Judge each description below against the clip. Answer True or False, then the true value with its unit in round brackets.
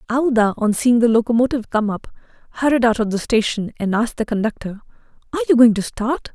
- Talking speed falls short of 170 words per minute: False (200 wpm)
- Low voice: False (230 Hz)